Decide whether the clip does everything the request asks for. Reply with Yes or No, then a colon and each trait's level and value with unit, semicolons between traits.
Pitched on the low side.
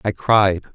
Yes: low, 100 Hz